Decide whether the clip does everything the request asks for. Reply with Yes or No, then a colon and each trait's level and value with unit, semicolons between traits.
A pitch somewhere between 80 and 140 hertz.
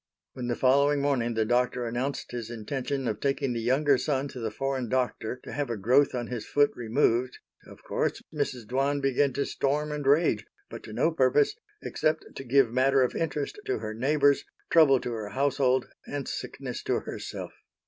Yes: low, 135 Hz